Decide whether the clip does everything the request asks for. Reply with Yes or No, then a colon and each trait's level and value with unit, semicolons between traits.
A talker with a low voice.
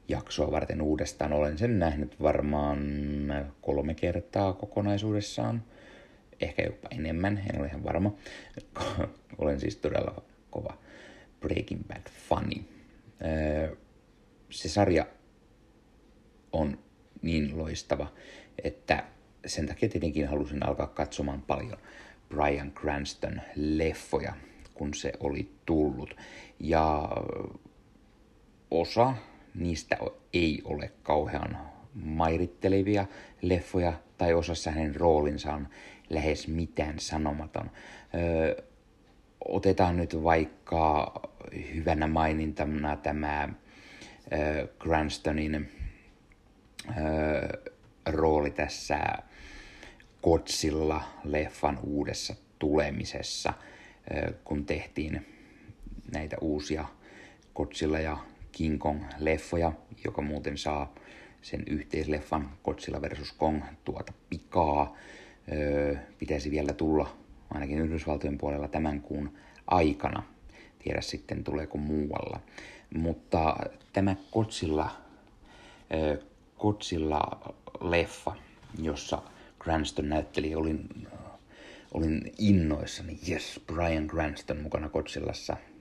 Yes: very low, 75 Hz